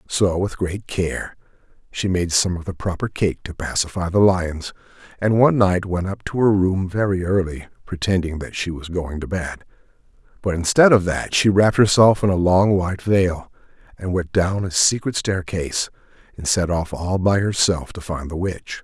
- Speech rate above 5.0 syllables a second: No, 4.8 syllables/s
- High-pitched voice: No, very low, 90 Hz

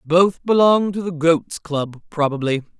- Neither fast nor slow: Yes, average, 150 wpm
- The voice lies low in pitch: No, medium, 170 Hz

